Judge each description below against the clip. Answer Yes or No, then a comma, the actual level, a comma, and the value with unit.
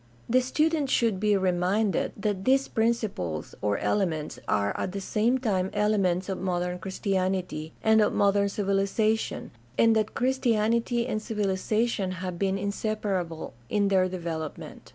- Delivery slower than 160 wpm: Yes, average, 140 wpm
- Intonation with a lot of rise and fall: No, average, 3.1 semitones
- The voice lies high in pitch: Yes, high, 200 Hz